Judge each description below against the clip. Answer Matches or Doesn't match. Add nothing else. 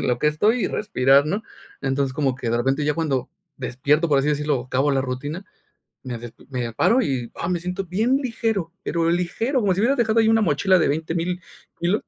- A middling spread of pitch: Doesn't match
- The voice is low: Doesn't match